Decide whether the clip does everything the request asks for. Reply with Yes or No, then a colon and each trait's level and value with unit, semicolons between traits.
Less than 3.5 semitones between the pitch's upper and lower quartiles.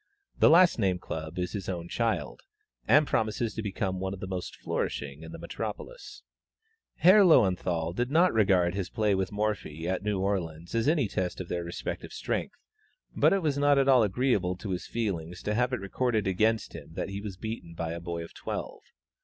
No: average, 4.8 semitones